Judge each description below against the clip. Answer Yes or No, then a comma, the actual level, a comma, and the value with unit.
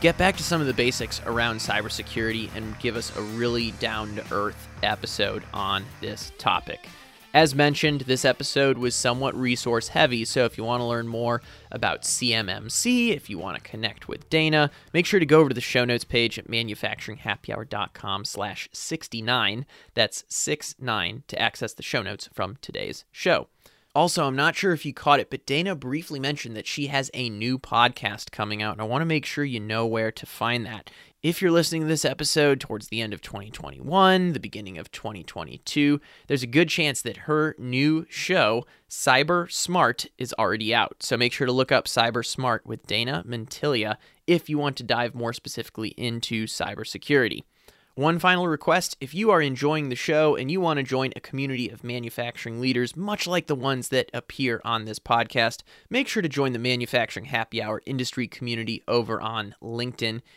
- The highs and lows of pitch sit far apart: No, average, 4.5 semitones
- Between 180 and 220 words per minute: Yes, average, 190 wpm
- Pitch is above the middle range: No, low, 125 Hz